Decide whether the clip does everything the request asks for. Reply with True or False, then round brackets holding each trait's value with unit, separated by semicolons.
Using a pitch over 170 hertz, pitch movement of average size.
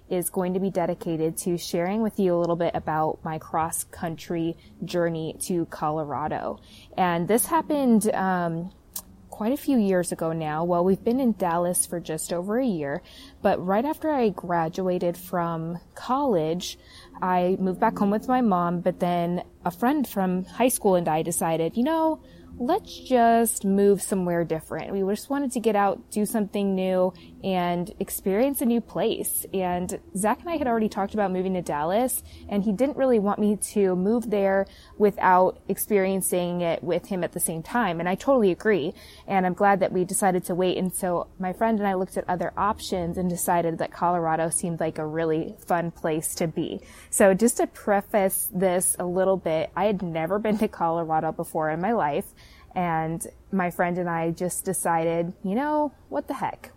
True (185 Hz; 3.6 semitones)